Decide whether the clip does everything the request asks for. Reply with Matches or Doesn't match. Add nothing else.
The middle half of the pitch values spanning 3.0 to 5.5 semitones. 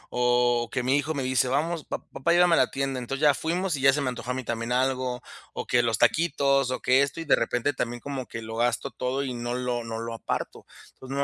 Doesn't match